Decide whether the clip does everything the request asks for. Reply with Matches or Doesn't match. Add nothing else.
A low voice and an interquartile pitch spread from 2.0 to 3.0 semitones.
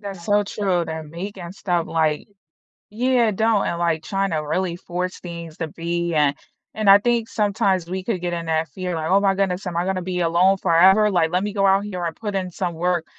Doesn't match